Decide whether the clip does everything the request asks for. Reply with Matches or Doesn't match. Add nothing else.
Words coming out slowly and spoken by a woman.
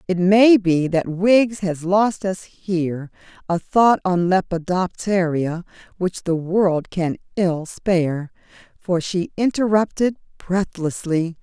Matches